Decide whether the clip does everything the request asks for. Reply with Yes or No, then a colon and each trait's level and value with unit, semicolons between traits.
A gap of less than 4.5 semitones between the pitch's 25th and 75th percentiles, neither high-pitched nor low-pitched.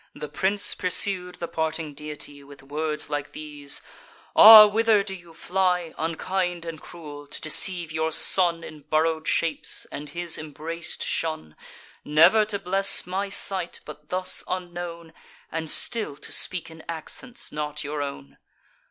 Yes: average, 3.3 semitones; medium, 165 Hz